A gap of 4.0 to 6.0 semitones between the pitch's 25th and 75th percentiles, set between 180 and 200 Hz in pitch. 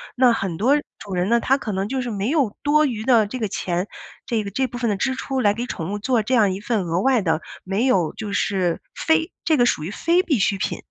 No: average, 5.0 semitones; high, 220 Hz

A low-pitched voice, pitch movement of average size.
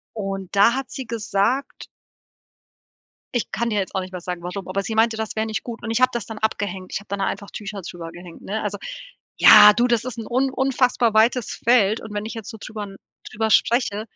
No: high, 215 Hz; average, 3.0 semitones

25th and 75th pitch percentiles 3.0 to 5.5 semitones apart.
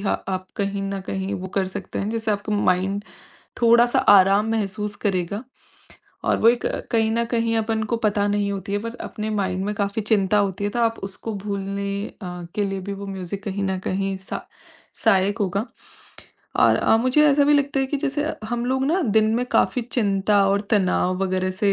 No: narrow, 2.6 semitones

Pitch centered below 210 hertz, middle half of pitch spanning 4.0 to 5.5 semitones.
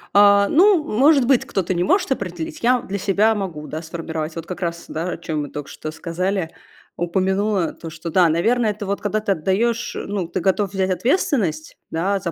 Yes: high, 190 Hz; average, 4.3 semitones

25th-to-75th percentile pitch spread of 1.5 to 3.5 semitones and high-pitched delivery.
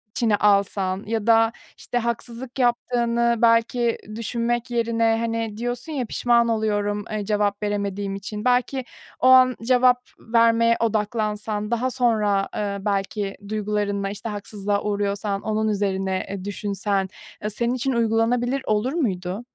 Yes: narrow, 2.6 semitones; high, 220 Hz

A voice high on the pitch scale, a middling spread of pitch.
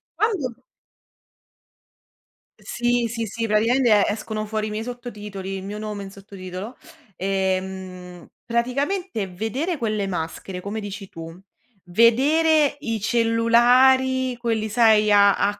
Yes: high, 220 Hz; average, 3.6 semitones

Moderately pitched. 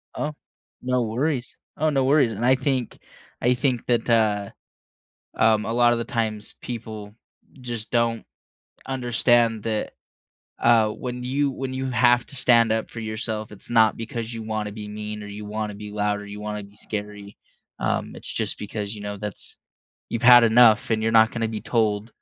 No: low, 115 Hz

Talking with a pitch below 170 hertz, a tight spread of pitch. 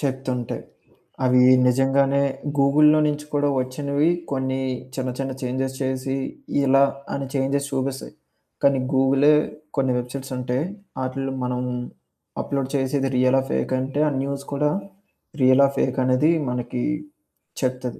Yes: low, 135 Hz; narrow, 1.3 semitones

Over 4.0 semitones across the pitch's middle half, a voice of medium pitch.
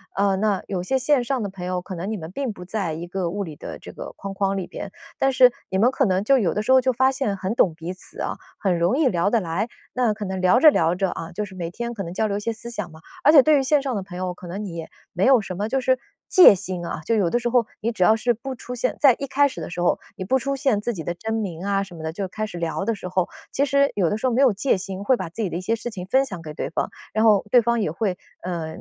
No: average, 5.1 semitones; high, 205 Hz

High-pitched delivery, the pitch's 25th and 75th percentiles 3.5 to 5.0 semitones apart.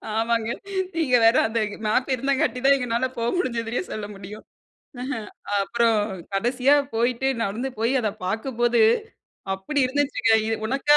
No: high, 235 Hz; average, 2.9 semitones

